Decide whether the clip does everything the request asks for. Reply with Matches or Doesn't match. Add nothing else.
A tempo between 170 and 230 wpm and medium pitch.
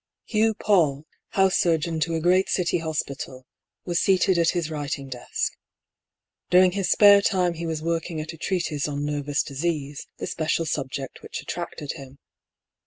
Doesn't match